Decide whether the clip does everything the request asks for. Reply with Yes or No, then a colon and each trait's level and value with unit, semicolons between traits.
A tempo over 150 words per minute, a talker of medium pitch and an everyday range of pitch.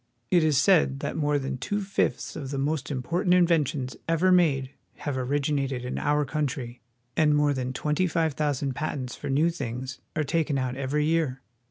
Yes: average, 185 wpm; medium, 145 Hz; average, 3.2 semitones